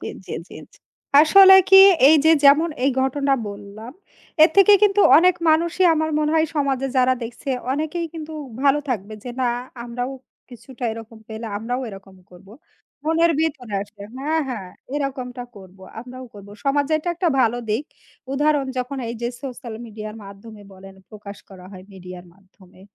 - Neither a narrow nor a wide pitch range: No, wide, 6.3 semitones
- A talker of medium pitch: No, very high, 255 Hz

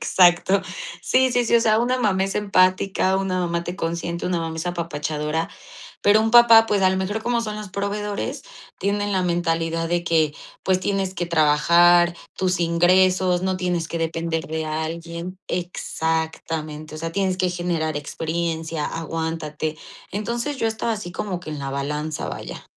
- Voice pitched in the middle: Yes, medium, 175 Hz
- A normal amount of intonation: Yes, average, 3.0 semitones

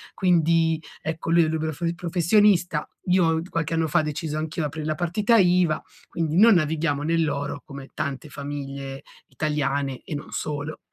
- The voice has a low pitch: No, medium, 160 Hz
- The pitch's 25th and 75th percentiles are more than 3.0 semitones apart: No, narrow, 2.5 semitones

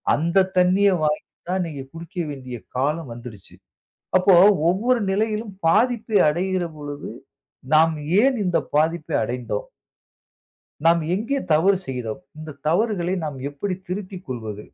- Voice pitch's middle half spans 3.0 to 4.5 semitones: No, average, 5.2 semitones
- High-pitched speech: No, medium, 170 Hz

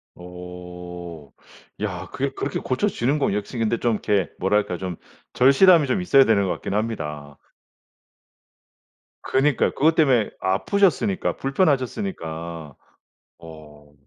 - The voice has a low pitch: Yes, low, 105 Hz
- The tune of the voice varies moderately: No, wide, 7.6 semitones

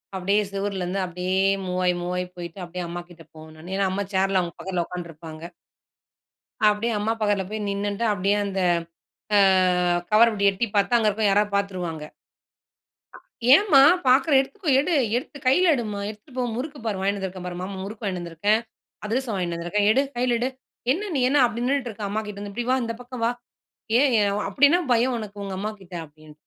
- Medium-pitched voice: No, high, 200 Hz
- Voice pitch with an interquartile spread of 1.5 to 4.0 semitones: No, average, 4.4 semitones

